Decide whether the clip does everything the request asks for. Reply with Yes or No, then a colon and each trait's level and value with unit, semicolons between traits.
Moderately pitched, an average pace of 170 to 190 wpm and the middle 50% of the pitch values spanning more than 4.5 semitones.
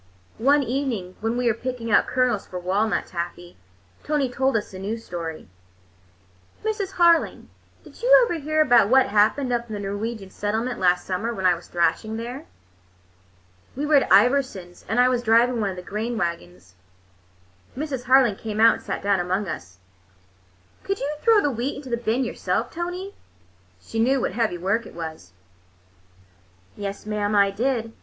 No: high, 225 Hz; average, 175 wpm; average, 5.1 semitones